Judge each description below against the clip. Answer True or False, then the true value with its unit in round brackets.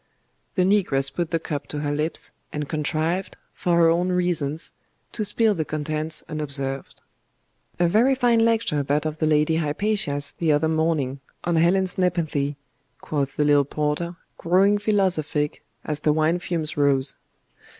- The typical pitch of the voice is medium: True (160 Hz)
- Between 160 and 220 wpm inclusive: False (150 wpm)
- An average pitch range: True (3.3 semitones)